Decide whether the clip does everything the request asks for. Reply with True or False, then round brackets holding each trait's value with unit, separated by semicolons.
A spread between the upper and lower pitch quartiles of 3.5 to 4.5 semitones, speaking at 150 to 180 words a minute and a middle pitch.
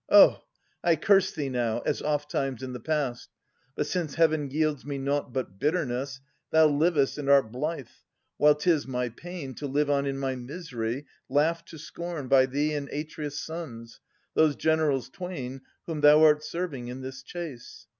False (3.1 semitones; 170 wpm; 145 Hz)